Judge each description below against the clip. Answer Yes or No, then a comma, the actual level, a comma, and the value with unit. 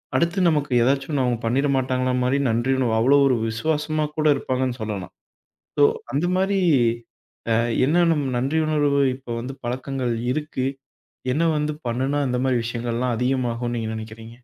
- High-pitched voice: No, low, 130 Hz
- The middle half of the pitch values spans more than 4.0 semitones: No, average, 3.4 semitones